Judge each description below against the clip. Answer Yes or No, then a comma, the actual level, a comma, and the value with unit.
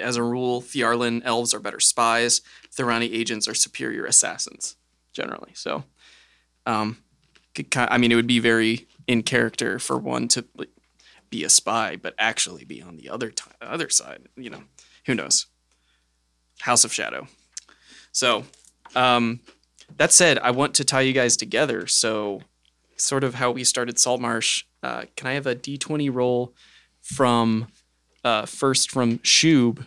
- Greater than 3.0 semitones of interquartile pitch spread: No, average, 2.7 semitones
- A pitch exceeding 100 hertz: Yes, low, 120 Hz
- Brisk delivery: No, average, 155 wpm